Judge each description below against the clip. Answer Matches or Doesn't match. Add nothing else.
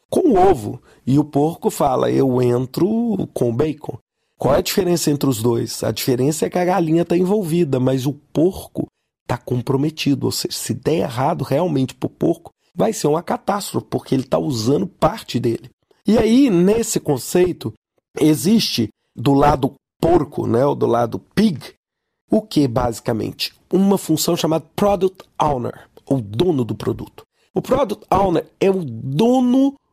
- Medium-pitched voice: Matches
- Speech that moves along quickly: Doesn't match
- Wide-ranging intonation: Matches